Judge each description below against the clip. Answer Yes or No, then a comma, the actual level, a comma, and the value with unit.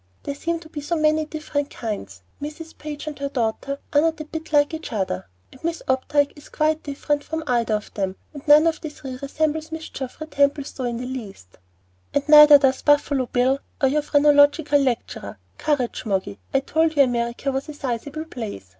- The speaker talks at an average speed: Yes, average, 195 wpm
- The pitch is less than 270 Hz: No, very high, 285 Hz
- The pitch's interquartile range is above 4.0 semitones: No, average, 3.3 semitones